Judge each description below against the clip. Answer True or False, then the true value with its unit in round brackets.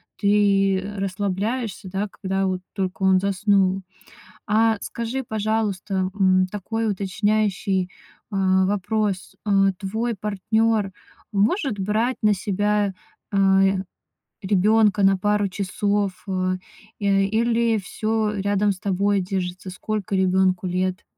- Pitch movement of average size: False (1.9 semitones)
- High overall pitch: True (200 Hz)